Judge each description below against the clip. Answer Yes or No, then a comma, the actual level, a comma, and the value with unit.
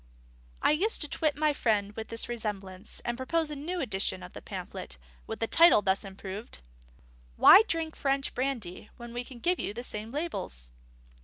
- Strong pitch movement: Yes, wide, 6.5 semitones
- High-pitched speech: Yes, high, 240 Hz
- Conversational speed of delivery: Yes, average, 175 wpm